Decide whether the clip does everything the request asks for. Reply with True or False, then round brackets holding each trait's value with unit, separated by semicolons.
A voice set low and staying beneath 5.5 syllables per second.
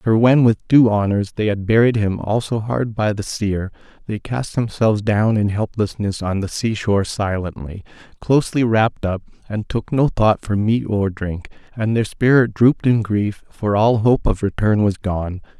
True (105 Hz; 4.6 syllables/s)